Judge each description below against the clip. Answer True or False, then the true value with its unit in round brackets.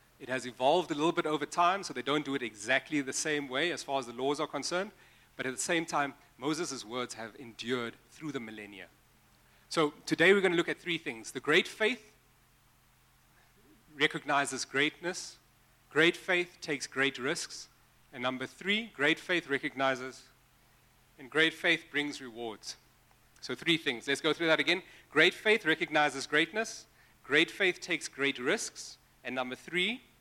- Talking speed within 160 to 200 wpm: True (170 wpm)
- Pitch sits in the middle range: True (145 Hz)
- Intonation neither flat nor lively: True (4.5 semitones)